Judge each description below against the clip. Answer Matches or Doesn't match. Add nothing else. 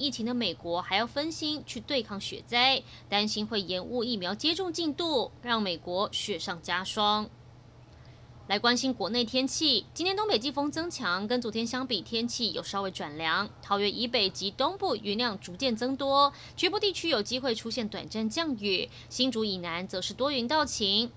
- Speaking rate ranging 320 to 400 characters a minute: Doesn't match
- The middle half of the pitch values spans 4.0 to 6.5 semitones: Matches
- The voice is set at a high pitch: Matches